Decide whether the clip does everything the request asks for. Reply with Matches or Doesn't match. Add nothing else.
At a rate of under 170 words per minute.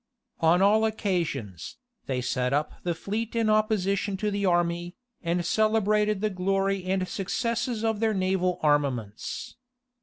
Matches